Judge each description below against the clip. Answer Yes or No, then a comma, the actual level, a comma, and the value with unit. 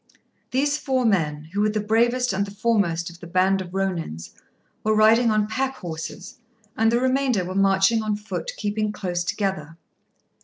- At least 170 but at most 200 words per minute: Yes, average, 175 wpm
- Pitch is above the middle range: Yes, high, 205 Hz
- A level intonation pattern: No, average, 3.8 semitones